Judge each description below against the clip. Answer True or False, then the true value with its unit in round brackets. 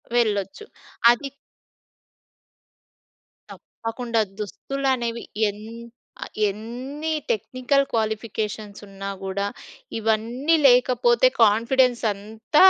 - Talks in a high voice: True (230 Hz)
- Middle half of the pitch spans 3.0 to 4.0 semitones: True (3.7 semitones)